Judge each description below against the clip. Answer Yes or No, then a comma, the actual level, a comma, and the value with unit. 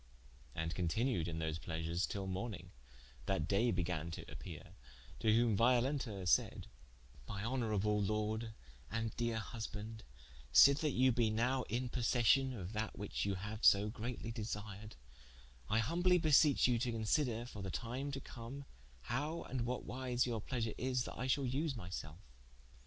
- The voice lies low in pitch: Yes, low, 115 Hz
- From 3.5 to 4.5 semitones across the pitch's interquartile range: Yes, average, 3.8 semitones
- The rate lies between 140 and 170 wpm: Yes, average, 160 wpm